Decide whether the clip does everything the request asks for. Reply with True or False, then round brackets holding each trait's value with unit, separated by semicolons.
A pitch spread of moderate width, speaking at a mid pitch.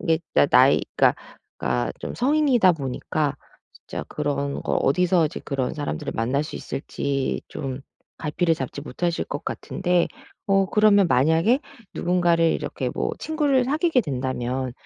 False (6.0 semitones; 160 Hz)